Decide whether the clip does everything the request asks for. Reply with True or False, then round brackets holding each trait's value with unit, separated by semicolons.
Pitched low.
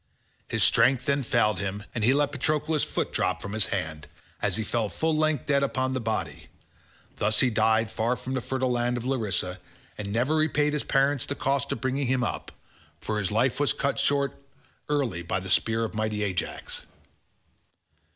True (120 Hz)